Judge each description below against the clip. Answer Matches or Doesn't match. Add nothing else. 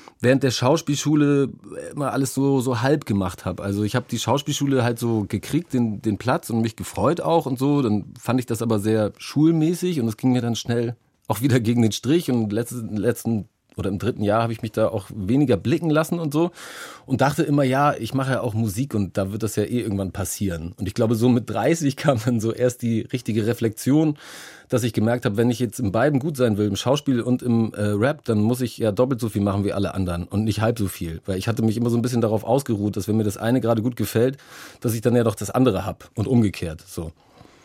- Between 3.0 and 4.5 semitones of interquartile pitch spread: Matches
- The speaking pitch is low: Matches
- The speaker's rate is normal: Doesn't match